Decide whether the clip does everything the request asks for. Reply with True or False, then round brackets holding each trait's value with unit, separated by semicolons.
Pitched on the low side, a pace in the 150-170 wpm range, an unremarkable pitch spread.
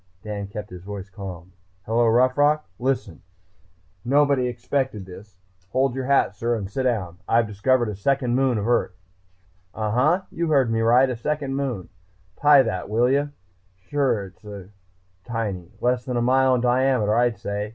True (120 Hz; 165 wpm; 4.3 semitones)